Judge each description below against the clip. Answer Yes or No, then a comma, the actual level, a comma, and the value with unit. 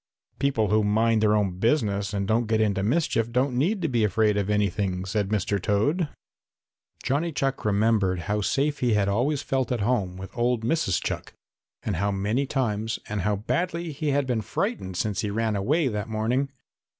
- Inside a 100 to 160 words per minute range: No, average, 185 wpm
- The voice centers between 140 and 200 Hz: No, low, 110 Hz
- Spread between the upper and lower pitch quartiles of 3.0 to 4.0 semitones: No, average, 4.5 semitones